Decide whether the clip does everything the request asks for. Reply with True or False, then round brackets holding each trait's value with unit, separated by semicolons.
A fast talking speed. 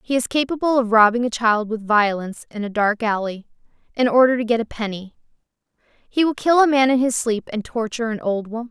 True (220 wpm)